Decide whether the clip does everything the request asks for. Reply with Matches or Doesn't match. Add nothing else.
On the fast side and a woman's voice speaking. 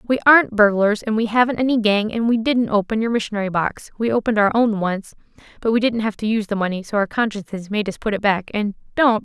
Matches